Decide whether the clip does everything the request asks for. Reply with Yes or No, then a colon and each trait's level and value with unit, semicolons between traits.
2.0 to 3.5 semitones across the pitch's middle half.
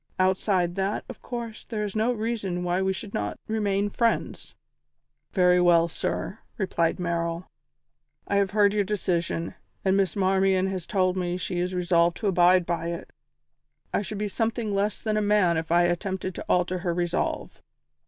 Yes: average, 2.8 semitones